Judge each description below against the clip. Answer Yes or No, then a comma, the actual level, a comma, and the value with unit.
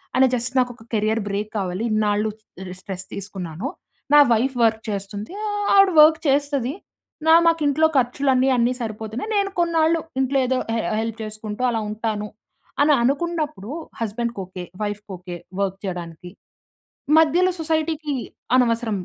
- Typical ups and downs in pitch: No, wide, 5.8 semitones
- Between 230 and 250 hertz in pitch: Yes, high, 235 Hz